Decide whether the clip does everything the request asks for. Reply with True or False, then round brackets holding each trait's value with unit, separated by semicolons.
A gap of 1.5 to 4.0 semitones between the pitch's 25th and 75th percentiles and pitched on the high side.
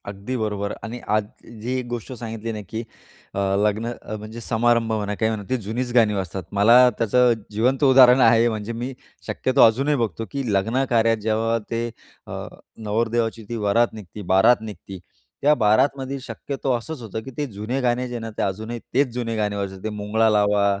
False (2.6 semitones; 115 Hz)